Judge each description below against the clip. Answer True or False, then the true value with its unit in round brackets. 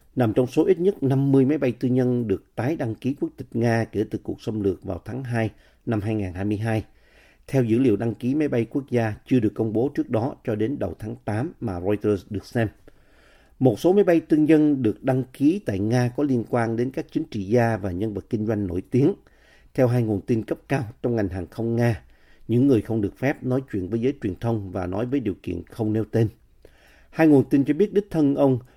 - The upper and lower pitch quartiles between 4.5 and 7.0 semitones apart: False (4.0 semitones)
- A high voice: False (120 Hz)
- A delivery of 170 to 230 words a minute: False (240 wpm)